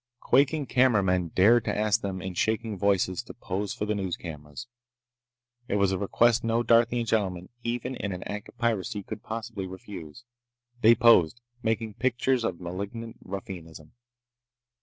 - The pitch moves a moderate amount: Yes, average, 3.9 semitones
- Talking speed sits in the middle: Yes, average, 155 wpm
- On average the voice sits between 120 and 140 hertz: No, low, 105 Hz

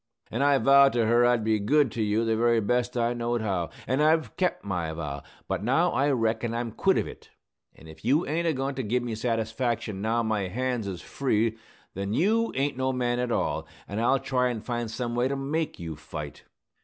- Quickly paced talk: Yes, fast, 220 wpm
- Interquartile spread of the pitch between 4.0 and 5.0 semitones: No, average, 3.4 semitones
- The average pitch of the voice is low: Yes, low, 120 Hz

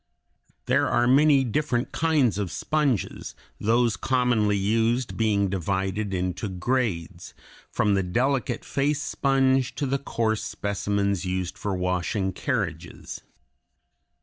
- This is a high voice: No, low, 110 Hz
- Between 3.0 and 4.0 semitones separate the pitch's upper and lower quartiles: No, average, 5.2 semitones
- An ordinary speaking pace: No, slow, 115 wpm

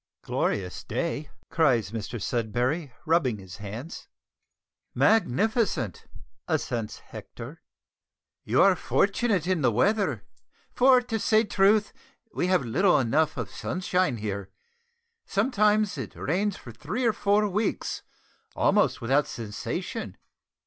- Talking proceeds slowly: Yes, slow, 115 wpm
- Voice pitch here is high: No, medium, 160 Hz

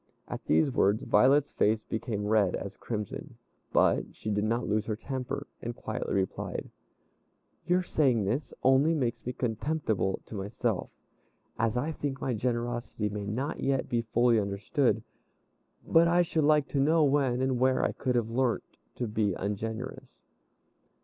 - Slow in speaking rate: No, average, 155 wpm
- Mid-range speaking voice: No, low, 120 Hz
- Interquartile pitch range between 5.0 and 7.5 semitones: No, average, 4.3 semitones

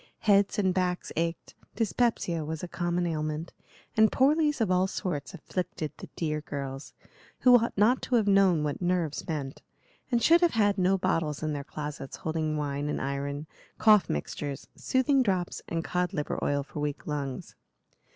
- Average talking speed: Yes, average, 170 wpm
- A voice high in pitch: No, medium, 170 Hz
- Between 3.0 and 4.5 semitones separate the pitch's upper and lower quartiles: No, wide, 5.4 semitones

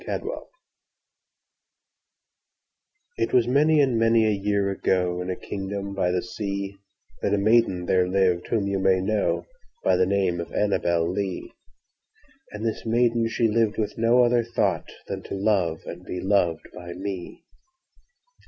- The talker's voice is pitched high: No, low, 100 Hz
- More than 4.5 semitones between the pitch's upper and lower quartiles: No, average, 3.6 semitones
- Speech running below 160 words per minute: Yes, average, 140 wpm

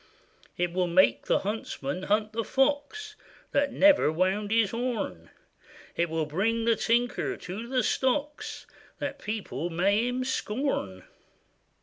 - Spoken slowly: Yes, slow, 130 wpm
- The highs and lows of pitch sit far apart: Yes, wide, 6.0 semitones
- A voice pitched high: Yes, high, 220 Hz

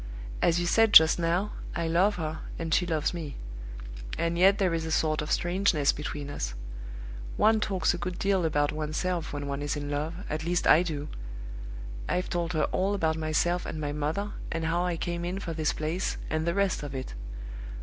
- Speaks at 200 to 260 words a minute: Yes, fast, 205 wpm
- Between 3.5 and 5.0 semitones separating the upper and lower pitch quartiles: No, narrow, 2.6 semitones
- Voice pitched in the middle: Yes, medium, 165 Hz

